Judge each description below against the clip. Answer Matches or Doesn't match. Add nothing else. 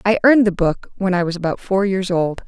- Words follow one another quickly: Matches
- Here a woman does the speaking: Matches